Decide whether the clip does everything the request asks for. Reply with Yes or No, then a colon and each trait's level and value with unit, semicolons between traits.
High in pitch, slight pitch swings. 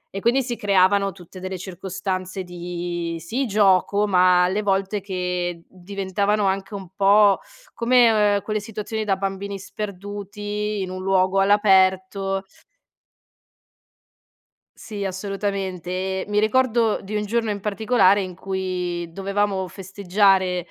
Yes: high, 195 Hz; narrow, 1.8 semitones